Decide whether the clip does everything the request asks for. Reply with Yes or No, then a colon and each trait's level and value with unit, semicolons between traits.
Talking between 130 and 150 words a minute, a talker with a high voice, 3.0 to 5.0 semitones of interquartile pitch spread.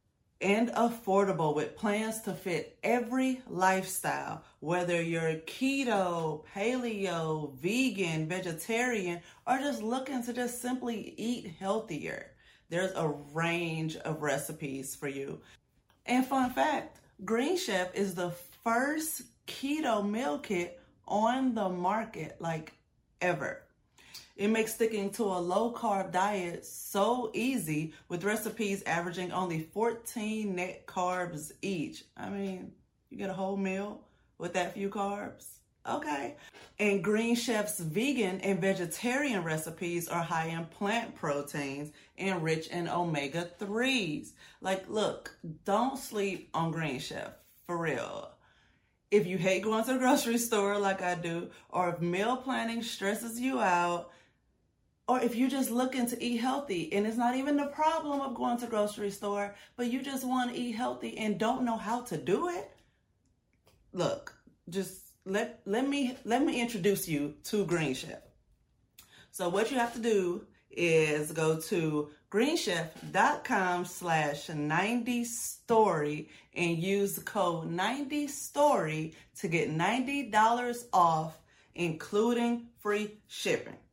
No: slow, 135 wpm; high, 200 Hz; wide, 5.5 semitones